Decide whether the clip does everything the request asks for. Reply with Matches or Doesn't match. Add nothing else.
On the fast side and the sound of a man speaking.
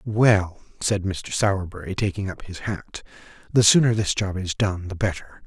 Doesn't match